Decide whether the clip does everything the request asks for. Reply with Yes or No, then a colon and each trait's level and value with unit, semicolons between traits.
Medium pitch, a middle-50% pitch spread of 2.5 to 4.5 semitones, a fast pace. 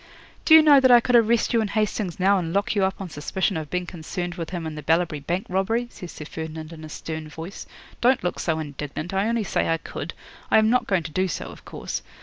No: medium, 180 Hz; average, 5.1 semitones; fast, 255 wpm